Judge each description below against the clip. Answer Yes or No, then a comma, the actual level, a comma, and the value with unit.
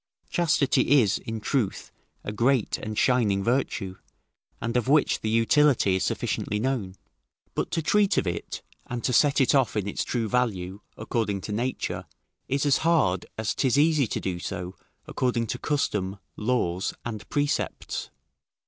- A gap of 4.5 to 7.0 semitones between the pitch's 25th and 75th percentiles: Yes, average, 5.0 semitones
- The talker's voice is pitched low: Yes, low, 115 Hz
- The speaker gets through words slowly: No, average, 155 wpm